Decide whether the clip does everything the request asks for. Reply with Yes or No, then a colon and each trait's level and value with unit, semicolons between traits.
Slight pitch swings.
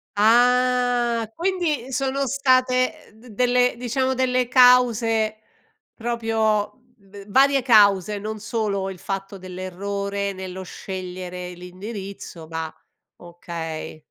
No: average, 4.7 semitones